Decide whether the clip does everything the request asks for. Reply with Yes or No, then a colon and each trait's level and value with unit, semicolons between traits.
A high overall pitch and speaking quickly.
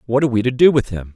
No: low, 120 Hz; fast, 365 wpm